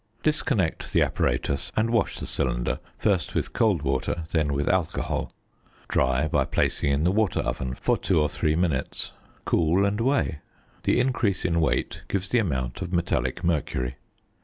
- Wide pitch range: Yes, wide, 6.2 semitones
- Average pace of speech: Yes, average, 160 wpm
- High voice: No, very low, 80 Hz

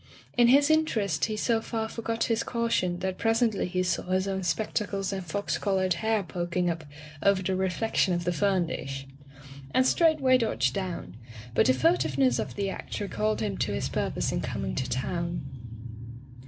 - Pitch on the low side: No, high, 190 Hz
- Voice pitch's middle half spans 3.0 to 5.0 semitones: Yes, average, 4.5 semitones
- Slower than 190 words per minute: Yes, average, 180 wpm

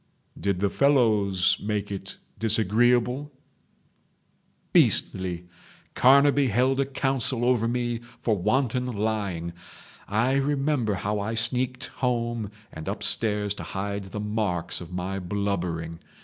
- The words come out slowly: Yes, slow, 110 wpm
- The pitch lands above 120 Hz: No, low, 110 Hz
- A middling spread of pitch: Yes, average, 4.1 semitones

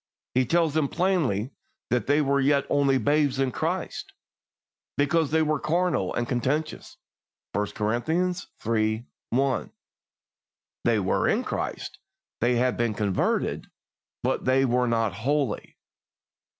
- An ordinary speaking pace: No, slow, 125 wpm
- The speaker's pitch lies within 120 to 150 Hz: Yes, low, 135 Hz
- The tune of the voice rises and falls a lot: No, average, 4.3 semitones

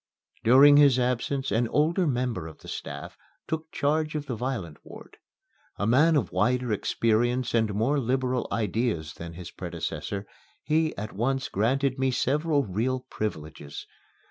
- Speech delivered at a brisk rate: No, average, 145 wpm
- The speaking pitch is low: Yes, low, 125 Hz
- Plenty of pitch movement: No, average, 4.7 semitones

